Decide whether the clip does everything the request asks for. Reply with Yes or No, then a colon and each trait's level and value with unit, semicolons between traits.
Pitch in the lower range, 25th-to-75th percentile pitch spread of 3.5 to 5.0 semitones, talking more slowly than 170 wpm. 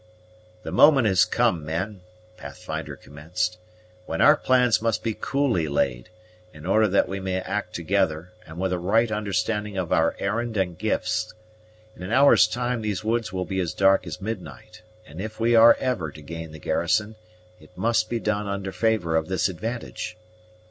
No: very low, 95 Hz; average, 4.3 semitones; average, 175 wpm